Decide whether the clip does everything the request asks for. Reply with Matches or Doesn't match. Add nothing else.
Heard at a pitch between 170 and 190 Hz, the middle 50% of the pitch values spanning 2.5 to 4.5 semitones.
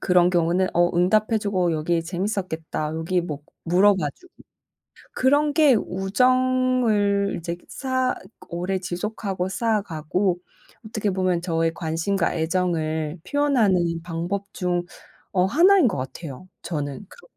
Matches